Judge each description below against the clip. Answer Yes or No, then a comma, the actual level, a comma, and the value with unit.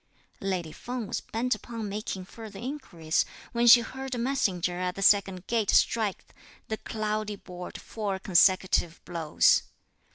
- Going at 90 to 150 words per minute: Yes, average, 140 wpm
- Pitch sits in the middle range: No, high, 205 Hz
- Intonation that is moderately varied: Yes, average, 4.1 semitones